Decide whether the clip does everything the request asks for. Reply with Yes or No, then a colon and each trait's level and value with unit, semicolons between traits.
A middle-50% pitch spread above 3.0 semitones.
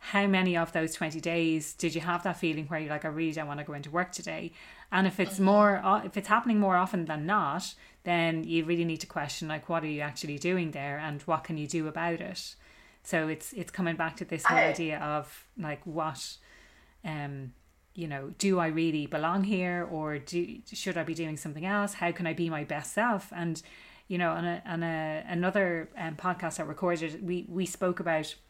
No: narrow, 2.6 semitones